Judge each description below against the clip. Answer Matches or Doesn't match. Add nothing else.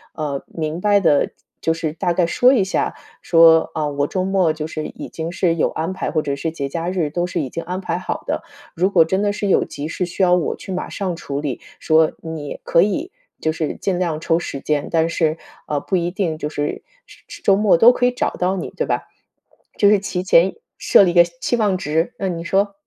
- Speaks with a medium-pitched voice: Matches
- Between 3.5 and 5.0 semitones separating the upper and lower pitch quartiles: Doesn't match